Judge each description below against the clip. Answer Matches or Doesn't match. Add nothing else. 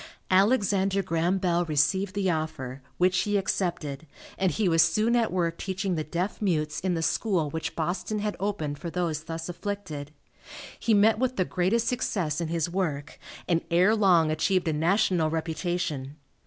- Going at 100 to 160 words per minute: Doesn't match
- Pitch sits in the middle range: Matches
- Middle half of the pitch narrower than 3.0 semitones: Doesn't match